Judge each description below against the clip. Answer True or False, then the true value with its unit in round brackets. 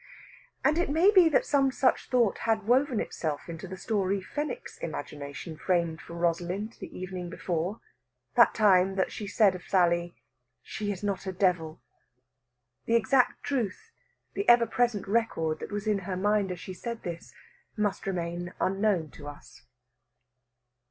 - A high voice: True (195 Hz)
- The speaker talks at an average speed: True (160 wpm)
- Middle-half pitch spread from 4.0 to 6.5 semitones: True (4.6 semitones)